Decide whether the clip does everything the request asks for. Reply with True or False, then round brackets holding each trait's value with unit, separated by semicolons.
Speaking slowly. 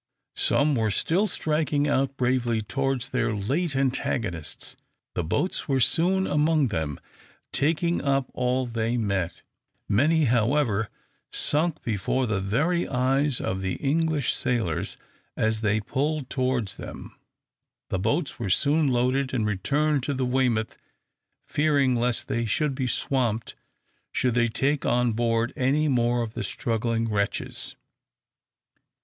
True (130 wpm)